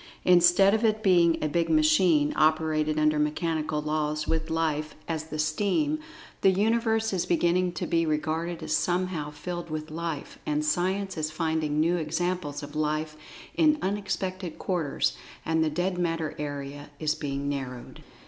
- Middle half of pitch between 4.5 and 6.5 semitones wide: No, average, 2.7 semitones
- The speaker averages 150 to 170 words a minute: Yes, average, 155 wpm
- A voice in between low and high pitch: Yes, medium, 160 Hz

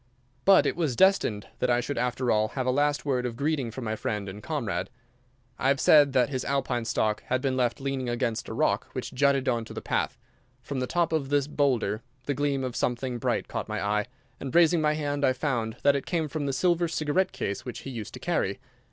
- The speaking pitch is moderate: No, low, 130 Hz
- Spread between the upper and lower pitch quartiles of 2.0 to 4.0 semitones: Yes, average, 3.3 semitones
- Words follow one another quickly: Yes, fast, 230 wpm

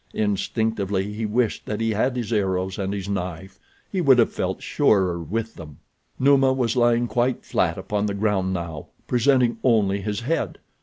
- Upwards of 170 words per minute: No, average, 165 wpm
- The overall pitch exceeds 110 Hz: No, low, 105 Hz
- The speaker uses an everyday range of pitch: Yes, average, 3.8 semitones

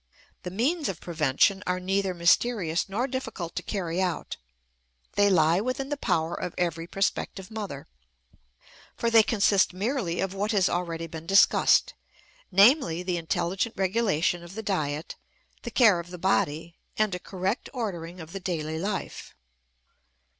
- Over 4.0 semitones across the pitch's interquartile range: No, average, 3.6 semitones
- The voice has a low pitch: No, medium, 185 Hz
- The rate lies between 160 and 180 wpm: No, average, 150 wpm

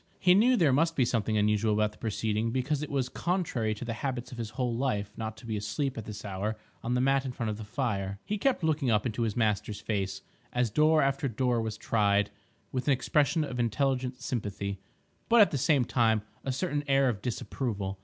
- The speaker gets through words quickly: Yes, fast, 220 wpm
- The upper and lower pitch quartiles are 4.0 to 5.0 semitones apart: Yes, average, 4.3 semitones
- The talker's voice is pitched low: Yes, low, 120 Hz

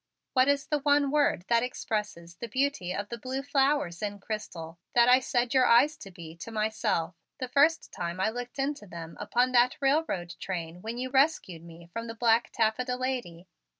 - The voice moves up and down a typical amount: No, wide, 6.3 semitones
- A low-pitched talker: No, high, 235 Hz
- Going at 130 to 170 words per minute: No, average, 190 wpm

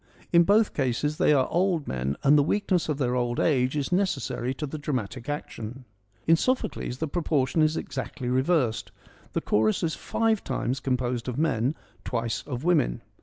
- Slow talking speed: No, average, 170 wpm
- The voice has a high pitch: No, low, 135 Hz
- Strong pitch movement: No, average, 4.6 semitones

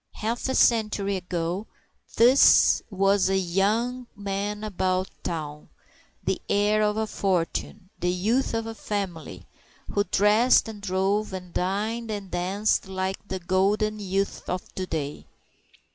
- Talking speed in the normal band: No, slow, 130 wpm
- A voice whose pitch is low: No, high, 195 Hz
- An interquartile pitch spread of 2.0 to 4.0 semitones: Yes, narrow, 2.4 semitones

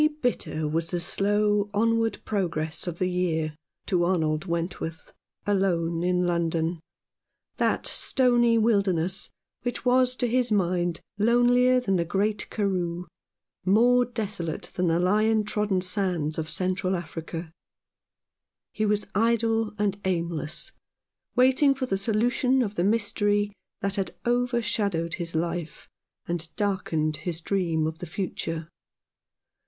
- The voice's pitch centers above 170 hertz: Yes, high, 190 Hz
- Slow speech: Yes, slow, 125 wpm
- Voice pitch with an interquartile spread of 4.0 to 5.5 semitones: Yes, average, 4.6 semitones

